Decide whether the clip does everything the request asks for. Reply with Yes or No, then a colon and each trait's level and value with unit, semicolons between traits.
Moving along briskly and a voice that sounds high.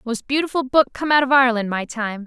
Yes: fast, 240 wpm; very high, 250 Hz